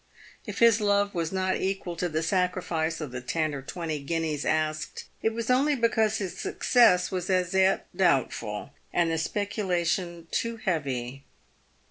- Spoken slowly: No, average, 155 wpm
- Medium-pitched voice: Yes, medium, 175 Hz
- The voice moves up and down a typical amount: Yes, average, 4.3 semitones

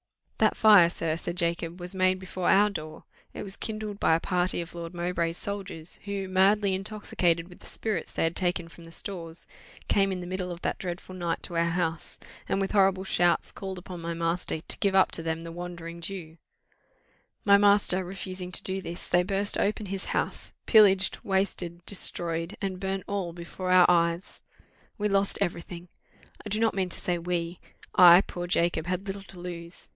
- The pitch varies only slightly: Yes, narrow, 2.3 semitones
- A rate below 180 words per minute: No, average, 195 wpm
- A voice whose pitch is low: No, medium, 180 Hz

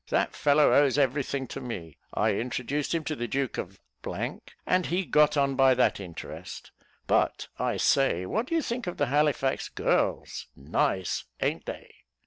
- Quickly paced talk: No, average, 170 wpm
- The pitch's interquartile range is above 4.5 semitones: No, average, 3.9 semitones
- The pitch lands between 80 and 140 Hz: Yes, low, 135 Hz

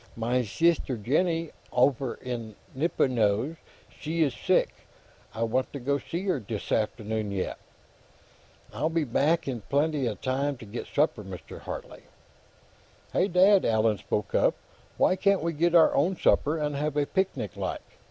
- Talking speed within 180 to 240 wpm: No, average, 150 wpm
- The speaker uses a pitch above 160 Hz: No, medium, 140 Hz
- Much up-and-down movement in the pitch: Yes, wide, 6.2 semitones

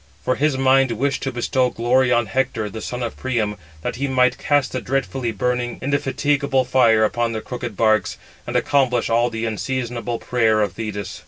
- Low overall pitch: Yes, low, 125 Hz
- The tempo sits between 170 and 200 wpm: Yes, average, 180 wpm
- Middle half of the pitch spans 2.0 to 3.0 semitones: Yes, narrow, 2.5 semitones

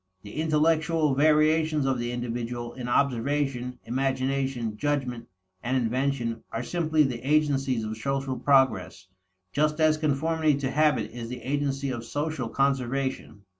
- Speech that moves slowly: Yes, slow, 130 wpm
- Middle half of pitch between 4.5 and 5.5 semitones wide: No, average, 3.6 semitones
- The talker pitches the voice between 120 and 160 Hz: Yes, low, 135 Hz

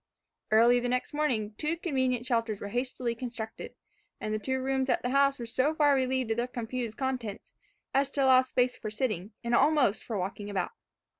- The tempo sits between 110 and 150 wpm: No, average, 195 wpm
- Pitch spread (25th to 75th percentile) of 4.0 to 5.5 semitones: No, average, 2.9 semitones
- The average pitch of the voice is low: No, very high, 250 Hz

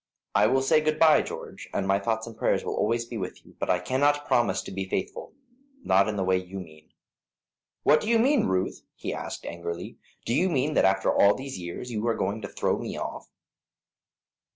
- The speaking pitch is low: Yes, low, 110 Hz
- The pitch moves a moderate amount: No, wide, 5.9 semitones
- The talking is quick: Yes, fast, 215 wpm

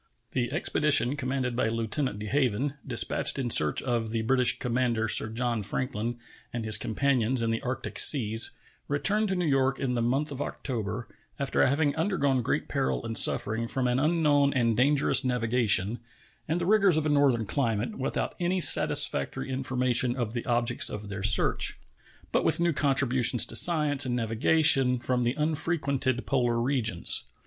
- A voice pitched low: Yes, low, 125 Hz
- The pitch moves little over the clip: No, average, 3.6 semitones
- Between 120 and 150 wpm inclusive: No, average, 165 wpm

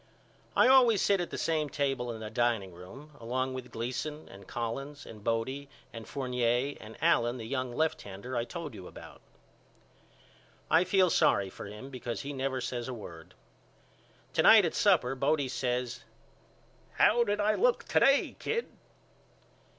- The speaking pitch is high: No, low, 130 Hz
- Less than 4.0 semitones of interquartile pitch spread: No, average, 4.5 semitones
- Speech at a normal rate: Yes, average, 160 wpm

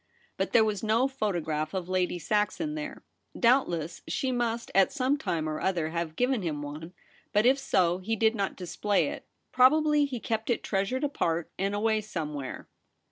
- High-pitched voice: Yes, high, 210 Hz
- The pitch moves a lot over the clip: Yes, wide, 6.6 semitones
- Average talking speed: Yes, average, 180 wpm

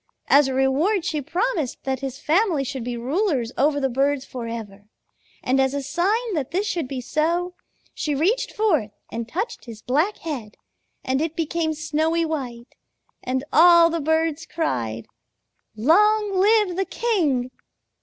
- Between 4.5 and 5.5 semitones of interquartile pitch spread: Yes, average, 5.1 semitones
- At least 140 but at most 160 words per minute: Yes, average, 155 wpm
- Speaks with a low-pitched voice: No, very high, 300 Hz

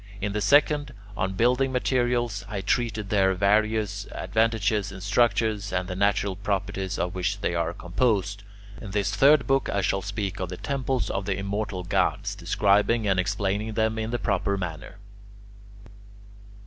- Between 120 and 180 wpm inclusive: Yes, average, 160 wpm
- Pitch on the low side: Yes, low, 100 Hz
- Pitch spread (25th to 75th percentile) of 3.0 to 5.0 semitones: No, narrow, 2.6 semitones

